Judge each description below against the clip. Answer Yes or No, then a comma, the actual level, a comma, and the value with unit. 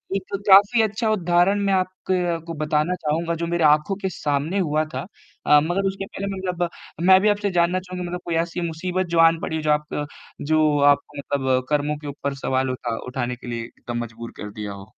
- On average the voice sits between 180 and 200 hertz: No, medium, 165 Hz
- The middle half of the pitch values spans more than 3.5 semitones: Yes, average, 4.4 semitones